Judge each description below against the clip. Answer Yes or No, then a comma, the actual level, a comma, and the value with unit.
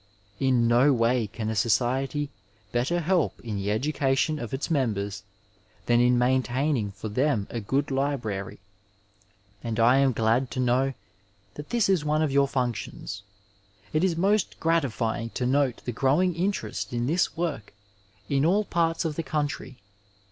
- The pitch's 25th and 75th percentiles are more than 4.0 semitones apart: Yes, average, 4.4 semitones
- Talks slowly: No, average, 155 wpm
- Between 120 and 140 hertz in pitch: Yes, low, 135 Hz